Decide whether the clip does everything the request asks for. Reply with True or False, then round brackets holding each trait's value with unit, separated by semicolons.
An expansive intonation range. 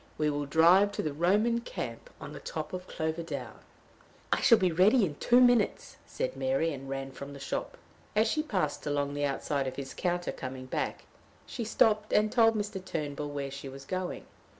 True (7.0 semitones)